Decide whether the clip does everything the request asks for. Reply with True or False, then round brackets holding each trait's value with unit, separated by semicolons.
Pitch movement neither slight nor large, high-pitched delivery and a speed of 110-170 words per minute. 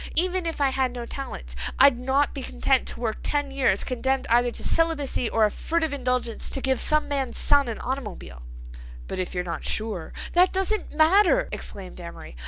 False (4.4 semitones; 265 Hz; 190 wpm)